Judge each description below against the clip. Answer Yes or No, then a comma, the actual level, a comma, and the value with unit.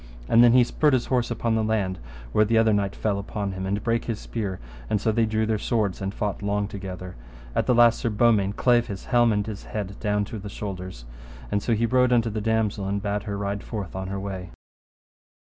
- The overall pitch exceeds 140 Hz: No, low, 105 Hz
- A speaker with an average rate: No, fast, 230 wpm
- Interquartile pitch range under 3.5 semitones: Yes, narrow, 2.5 semitones